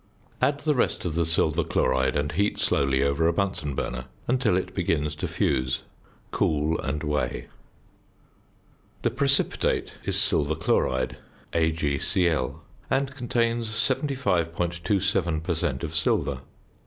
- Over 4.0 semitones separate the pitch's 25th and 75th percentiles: Yes, wide, 5.4 semitones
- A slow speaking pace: Yes, slow, 125 wpm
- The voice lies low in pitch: Yes, very low, 80 Hz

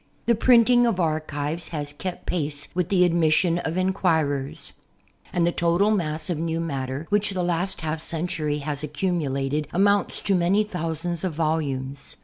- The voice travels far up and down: No, average, 3.3 semitones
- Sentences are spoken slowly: No, average, 160 wpm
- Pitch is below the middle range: No, medium, 165 Hz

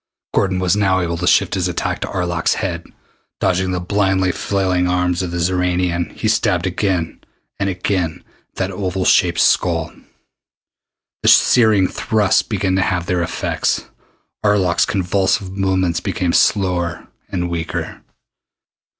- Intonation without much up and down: Yes, narrow, 1.6 semitones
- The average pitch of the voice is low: Yes, very low, 90 Hz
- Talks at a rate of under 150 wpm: Yes, average, 140 wpm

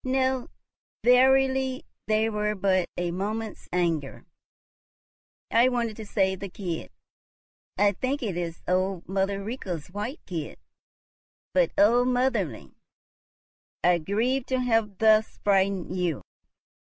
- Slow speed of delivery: Yes, slow, 115 wpm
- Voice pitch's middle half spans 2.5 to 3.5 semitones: No, average, 5.0 semitones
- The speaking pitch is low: No, high, 210 Hz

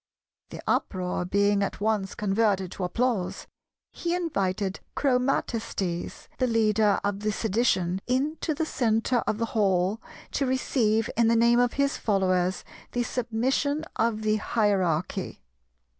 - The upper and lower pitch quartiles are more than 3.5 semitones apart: Yes, average, 4.0 semitones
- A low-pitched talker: No, high, 220 Hz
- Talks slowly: Yes, slow, 130 wpm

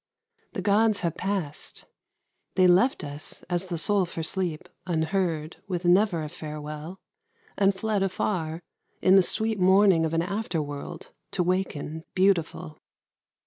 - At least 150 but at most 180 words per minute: No, average, 140 wpm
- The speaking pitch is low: No, medium, 180 Hz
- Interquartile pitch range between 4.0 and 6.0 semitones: No, average, 3.5 semitones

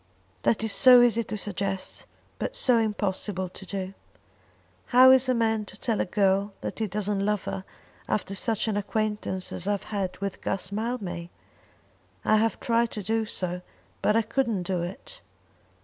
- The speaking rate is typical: Yes, average, 175 wpm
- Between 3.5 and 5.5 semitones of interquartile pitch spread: No, average, 2.8 semitones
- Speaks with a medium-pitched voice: No, high, 210 Hz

